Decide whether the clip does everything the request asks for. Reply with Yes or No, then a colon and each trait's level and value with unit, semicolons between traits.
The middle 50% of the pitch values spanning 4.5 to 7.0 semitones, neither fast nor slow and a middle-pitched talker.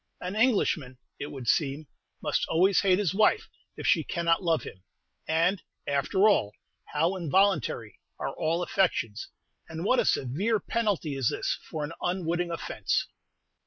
Yes: average, 4.8 semitones; average, 150 wpm; medium, 170 Hz